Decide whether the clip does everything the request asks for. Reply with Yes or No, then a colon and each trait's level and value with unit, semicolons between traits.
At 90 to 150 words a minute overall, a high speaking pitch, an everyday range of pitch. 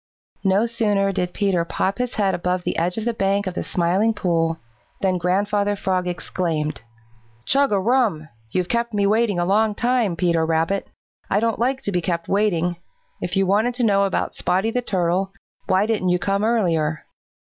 No: average, 185 wpm; high, 195 Hz; average, 3.4 semitones